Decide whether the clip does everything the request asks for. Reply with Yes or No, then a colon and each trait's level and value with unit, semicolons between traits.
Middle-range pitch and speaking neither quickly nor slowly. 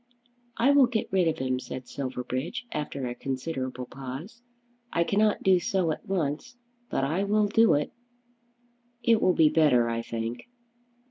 Yes: medium, 155 Hz; average, 155 wpm